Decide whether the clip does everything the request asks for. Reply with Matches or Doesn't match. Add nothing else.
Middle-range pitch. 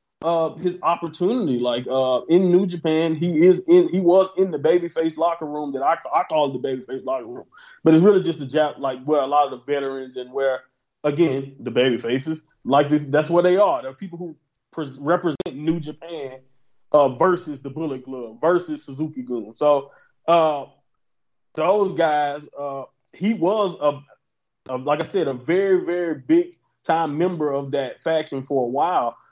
Matches